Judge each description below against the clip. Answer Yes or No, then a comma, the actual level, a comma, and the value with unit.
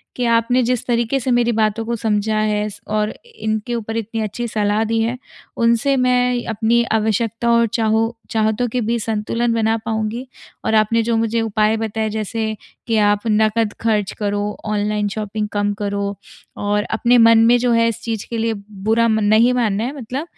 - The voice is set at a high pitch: Yes, high, 225 Hz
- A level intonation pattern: Yes, narrow, 1.6 semitones